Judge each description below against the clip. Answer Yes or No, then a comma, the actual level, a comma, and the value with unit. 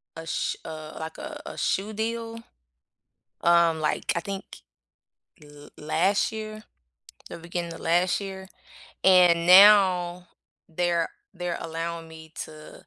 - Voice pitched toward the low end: No, medium, 175 Hz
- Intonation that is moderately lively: Yes, average, 3.1 semitones